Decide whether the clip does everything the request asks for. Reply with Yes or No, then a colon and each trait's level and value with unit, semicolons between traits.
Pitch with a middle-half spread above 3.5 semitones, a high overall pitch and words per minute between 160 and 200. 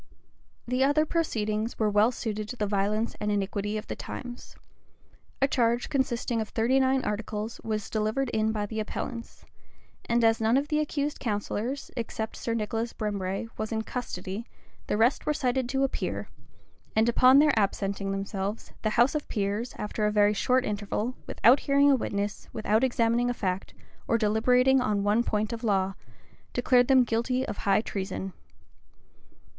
No: average, 3.2 semitones; high, 225 Hz; average, 165 wpm